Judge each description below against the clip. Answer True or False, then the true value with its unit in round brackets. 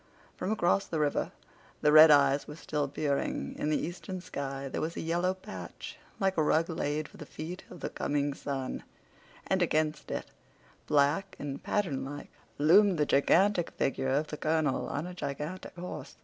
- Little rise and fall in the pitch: False (3.6 semitones)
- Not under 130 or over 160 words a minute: False (175 wpm)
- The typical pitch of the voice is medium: True (155 Hz)